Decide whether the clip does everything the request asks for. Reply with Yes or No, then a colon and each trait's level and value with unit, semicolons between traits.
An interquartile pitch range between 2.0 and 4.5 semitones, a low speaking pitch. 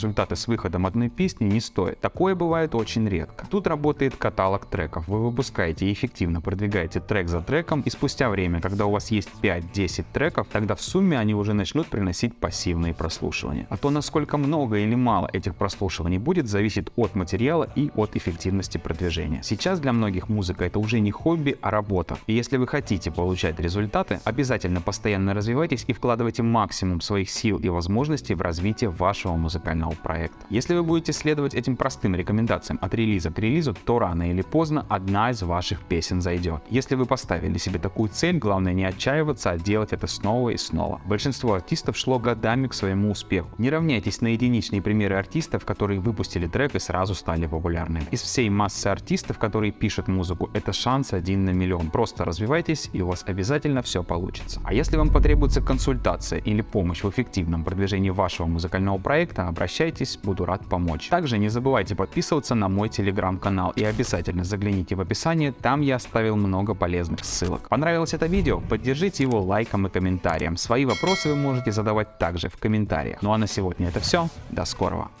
No: average, 5.1 semitones; low, 105 Hz